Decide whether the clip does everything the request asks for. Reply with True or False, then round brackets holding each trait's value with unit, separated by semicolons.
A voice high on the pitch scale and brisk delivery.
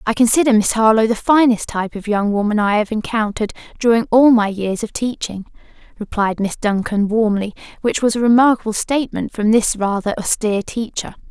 False (220 Hz; 175 wpm)